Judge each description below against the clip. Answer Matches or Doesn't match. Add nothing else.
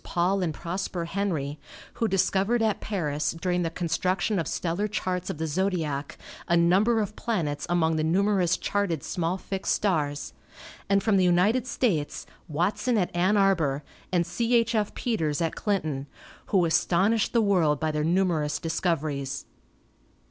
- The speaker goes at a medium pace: Matches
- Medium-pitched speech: Matches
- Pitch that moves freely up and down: Doesn't match